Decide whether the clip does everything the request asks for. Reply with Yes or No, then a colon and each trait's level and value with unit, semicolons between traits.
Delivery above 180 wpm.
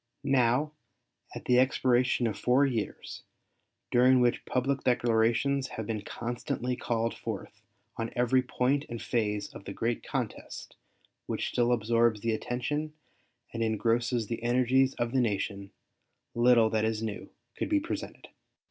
No: average, 140 wpm